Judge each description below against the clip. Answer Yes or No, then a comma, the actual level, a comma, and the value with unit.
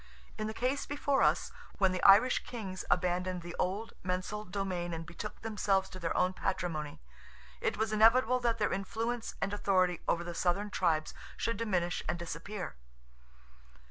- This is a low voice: No, high, 190 Hz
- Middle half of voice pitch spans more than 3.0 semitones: Yes, average, 3.6 semitones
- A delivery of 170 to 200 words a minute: No, average, 160 wpm